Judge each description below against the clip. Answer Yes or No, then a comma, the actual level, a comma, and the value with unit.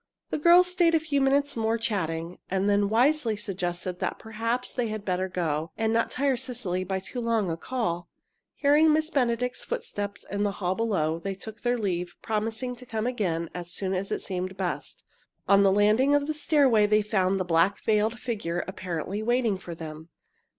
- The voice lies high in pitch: Yes, high, 210 Hz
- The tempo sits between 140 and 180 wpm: No, average, 190 wpm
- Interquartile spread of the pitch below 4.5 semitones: No, average, 5.0 semitones